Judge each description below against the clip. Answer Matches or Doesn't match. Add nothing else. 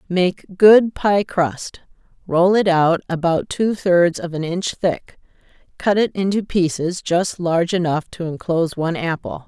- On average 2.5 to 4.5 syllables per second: Matches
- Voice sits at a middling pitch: Matches